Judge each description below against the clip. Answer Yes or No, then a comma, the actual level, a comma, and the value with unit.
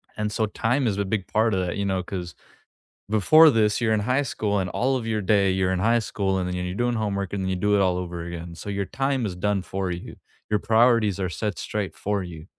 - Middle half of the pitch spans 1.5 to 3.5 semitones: Yes, average, 3.0 semitones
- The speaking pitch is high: No, low, 100 Hz